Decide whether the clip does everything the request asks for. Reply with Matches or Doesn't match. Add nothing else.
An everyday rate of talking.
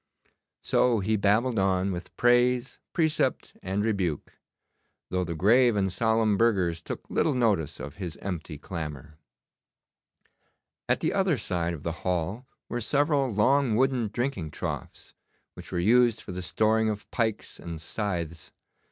Matches